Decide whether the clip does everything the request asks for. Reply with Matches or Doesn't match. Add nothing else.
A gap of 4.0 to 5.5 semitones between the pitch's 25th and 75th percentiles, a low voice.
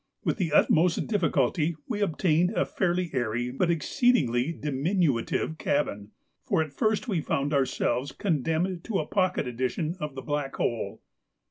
Doesn't match